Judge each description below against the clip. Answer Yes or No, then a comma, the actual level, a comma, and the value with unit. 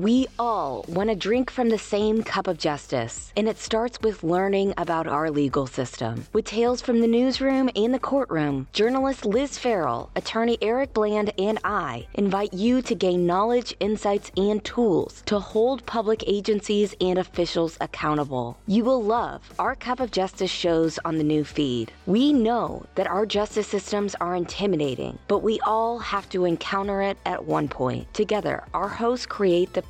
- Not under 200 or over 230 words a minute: No, average, 175 wpm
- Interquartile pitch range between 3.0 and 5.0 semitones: Yes, average, 4.3 semitones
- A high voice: Yes, high, 205 Hz